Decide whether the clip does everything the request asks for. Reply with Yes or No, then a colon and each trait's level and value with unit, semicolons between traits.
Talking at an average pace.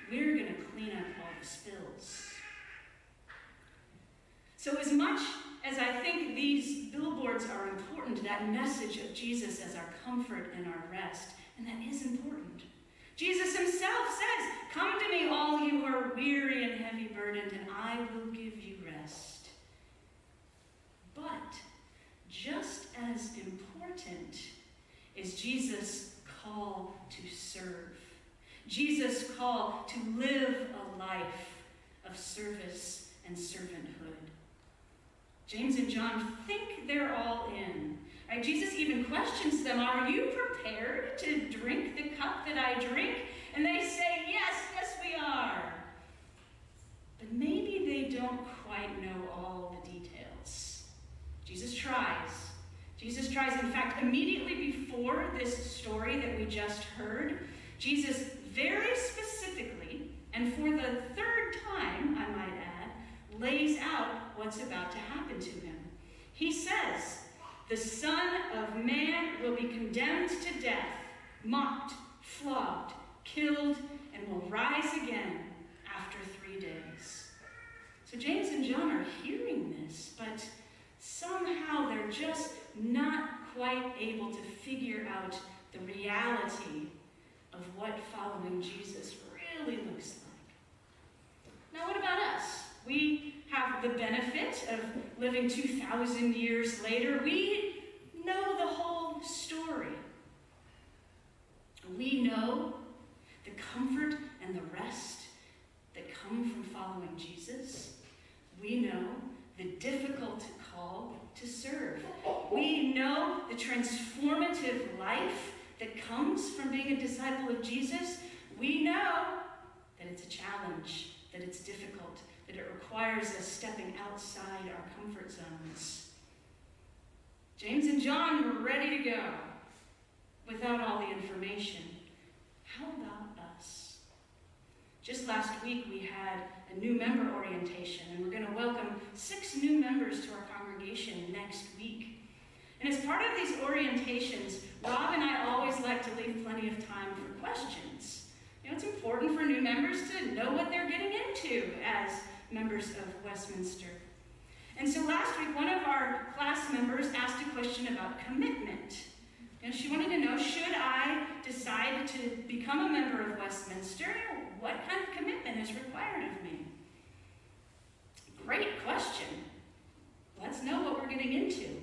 No: slow, 130 wpm